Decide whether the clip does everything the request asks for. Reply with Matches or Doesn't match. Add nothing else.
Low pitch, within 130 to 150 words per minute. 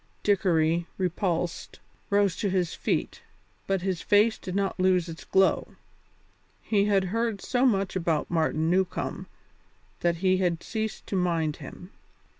Doesn't match